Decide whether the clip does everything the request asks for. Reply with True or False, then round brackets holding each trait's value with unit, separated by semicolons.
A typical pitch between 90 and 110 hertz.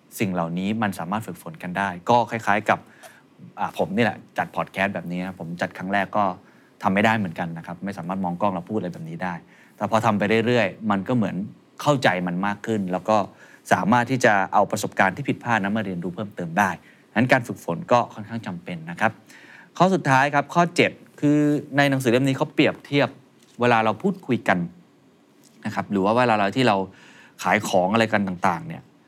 True (105 Hz)